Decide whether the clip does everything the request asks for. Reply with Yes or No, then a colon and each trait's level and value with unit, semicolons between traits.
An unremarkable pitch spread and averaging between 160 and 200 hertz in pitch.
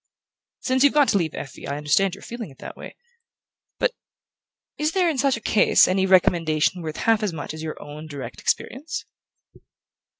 No: wide, 8.8 semitones; high, 190 Hz